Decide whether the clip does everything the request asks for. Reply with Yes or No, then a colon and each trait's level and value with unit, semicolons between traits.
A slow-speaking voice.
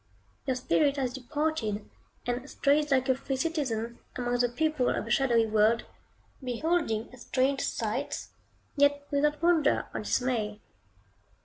Yes: slow, 130 wpm